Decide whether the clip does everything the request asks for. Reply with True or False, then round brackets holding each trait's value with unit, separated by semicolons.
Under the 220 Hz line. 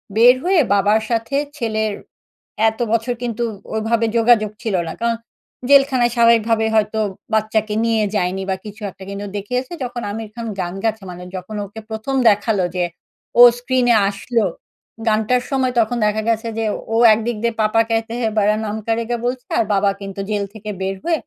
False (225 Hz)